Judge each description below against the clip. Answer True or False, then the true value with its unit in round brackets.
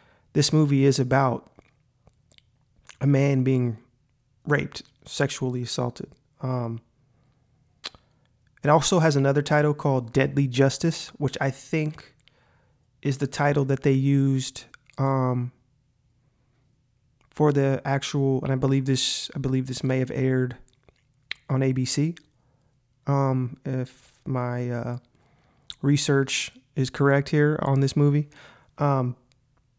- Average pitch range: False (1.6 semitones)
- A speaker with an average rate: False (115 wpm)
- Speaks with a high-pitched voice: False (135 Hz)